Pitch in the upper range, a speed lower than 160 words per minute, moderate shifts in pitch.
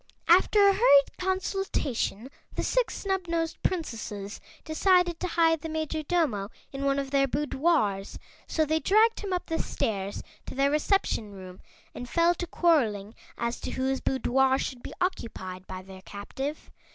No: very high, 290 Hz; average, 150 wpm; wide, 7.2 semitones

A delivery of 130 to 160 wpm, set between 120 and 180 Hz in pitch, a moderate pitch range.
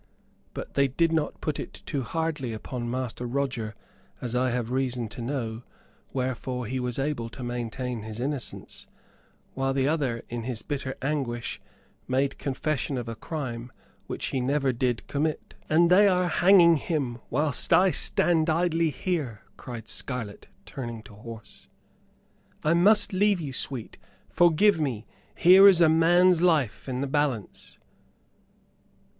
Yes: average, 150 wpm; low, 135 Hz; average, 4.9 semitones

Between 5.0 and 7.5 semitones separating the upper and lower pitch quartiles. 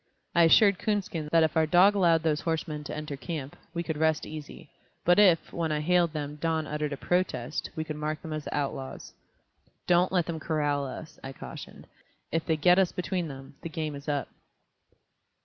No: narrow, 2.4 semitones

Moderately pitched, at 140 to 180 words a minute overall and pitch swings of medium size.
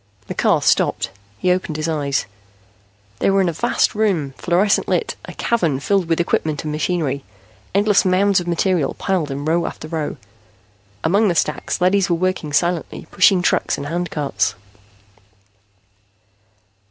Yes: medium, 170 Hz; average, 150 wpm; average, 3.5 semitones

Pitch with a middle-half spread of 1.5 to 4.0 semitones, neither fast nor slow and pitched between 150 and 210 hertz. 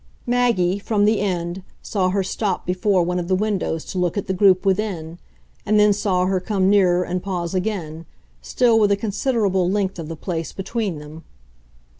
Yes: narrow, 2.6 semitones; average, 185 wpm; high, 190 Hz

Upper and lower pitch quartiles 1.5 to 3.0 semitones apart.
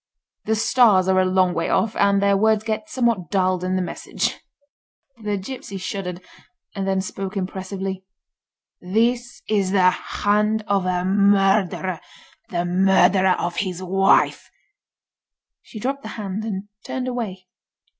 Yes: narrow, 2.5 semitones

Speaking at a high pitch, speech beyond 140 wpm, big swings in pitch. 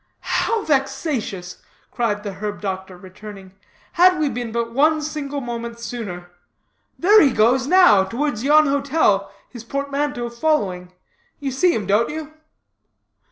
No: high, 240 Hz; slow, 135 wpm; wide, 6.1 semitones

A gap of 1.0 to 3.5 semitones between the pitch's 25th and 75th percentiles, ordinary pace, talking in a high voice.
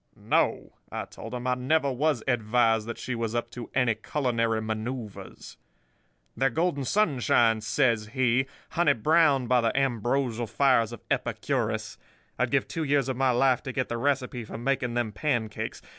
No: average, 2.8 semitones; average, 165 wpm; low, 125 Hz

